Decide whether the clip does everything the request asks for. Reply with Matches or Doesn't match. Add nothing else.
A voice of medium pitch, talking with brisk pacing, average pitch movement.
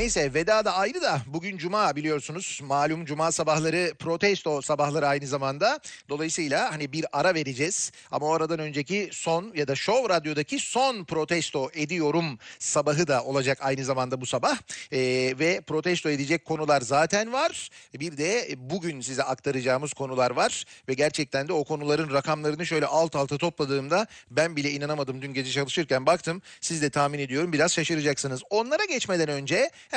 Matches